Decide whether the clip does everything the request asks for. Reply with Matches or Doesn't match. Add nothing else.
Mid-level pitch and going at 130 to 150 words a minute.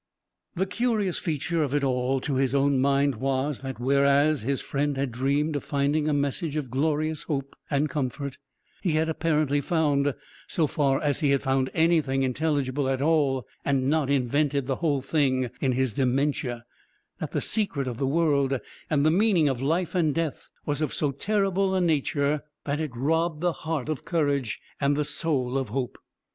Doesn't match